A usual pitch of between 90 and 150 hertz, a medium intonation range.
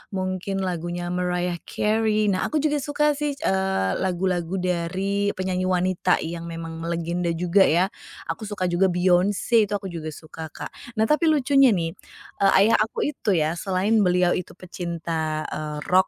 No: medium, 185 Hz; average, 3.0 semitones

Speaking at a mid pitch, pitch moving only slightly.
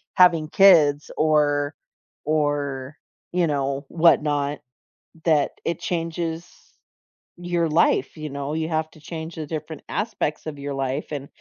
Yes: medium, 155 Hz; narrow, 2.3 semitones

